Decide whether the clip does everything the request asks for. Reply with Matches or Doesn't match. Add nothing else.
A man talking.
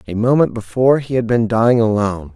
Matches